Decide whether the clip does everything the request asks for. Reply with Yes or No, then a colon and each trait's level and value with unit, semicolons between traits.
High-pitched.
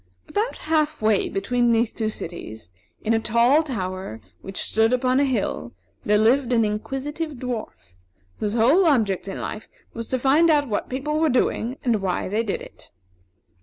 Yes: high, 235 Hz